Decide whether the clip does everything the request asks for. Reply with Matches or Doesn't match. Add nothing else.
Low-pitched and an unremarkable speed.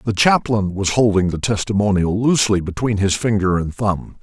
Matches